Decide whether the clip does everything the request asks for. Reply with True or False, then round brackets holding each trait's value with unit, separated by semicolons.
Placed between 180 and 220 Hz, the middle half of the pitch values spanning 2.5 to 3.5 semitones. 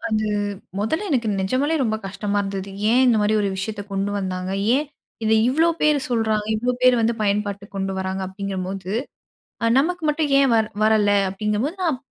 False (215 Hz; 4.3 semitones)